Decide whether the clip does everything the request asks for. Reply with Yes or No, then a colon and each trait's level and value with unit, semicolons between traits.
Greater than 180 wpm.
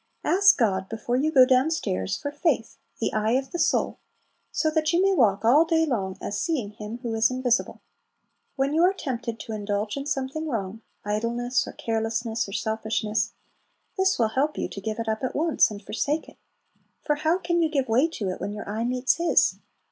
Yes: fast, 205 wpm